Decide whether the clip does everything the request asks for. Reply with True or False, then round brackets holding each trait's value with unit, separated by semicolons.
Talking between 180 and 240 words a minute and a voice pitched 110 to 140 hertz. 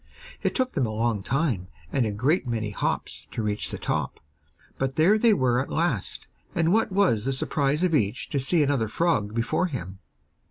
True (195 wpm; 135 Hz)